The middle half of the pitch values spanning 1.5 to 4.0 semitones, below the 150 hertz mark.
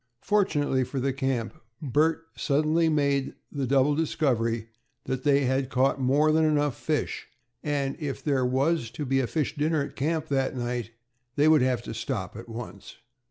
Yes: average, 2.9 semitones; medium, 140 Hz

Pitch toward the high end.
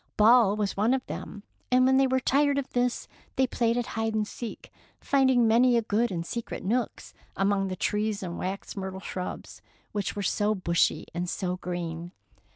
Yes: high, 215 Hz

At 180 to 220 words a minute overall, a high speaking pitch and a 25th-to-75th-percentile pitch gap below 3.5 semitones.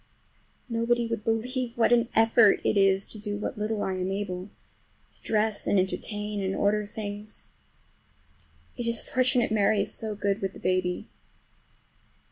No: average, 150 wpm; high, 210 Hz; narrow, 2.4 semitones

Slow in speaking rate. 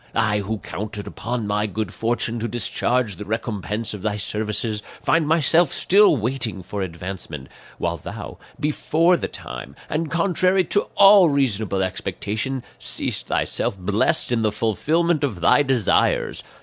No: average, 145 wpm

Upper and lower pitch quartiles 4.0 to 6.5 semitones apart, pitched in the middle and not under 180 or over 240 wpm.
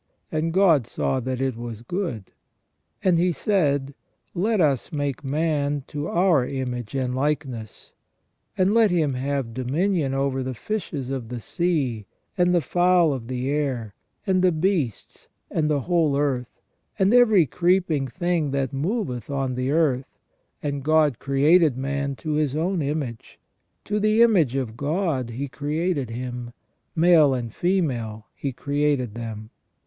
No: average, 5.1 semitones; medium, 145 Hz; average, 150 wpm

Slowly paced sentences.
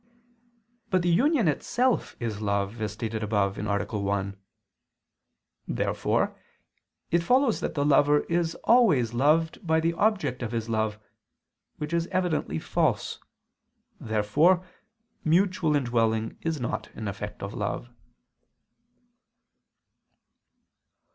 Yes: slow, 110 wpm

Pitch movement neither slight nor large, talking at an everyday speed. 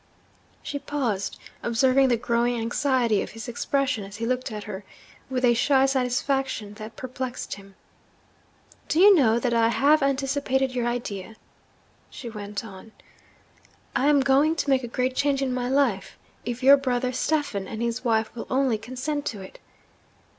Yes: average, 3.1 semitones; average, 165 wpm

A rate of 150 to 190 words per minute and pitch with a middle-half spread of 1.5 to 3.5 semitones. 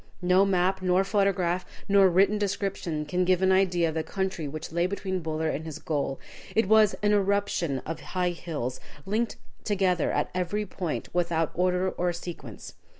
Yes: average, 170 wpm; average, 2.9 semitones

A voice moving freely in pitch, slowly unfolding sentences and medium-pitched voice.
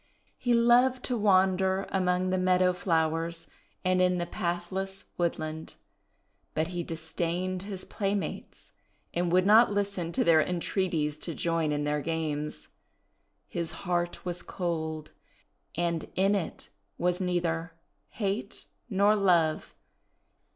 No: narrow, 2.6 semitones; slow, 125 wpm; medium, 180 Hz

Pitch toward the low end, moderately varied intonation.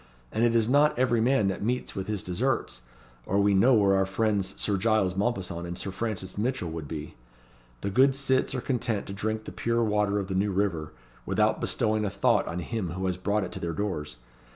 Yes: low, 100 Hz; average, 3.7 semitones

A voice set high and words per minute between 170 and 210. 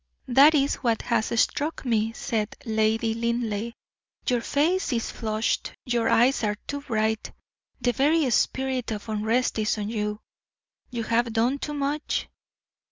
No: high, 235 Hz; average, 145 wpm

